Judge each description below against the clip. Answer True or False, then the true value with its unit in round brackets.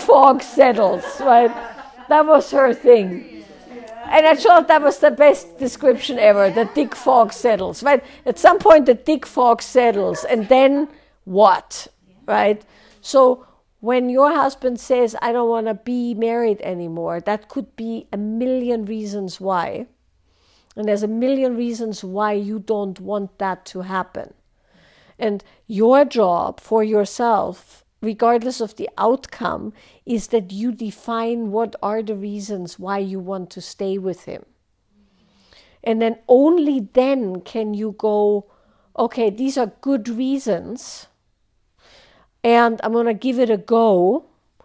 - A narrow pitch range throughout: False (3.8 semitones)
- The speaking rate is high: False (145 wpm)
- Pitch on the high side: True (230 Hz)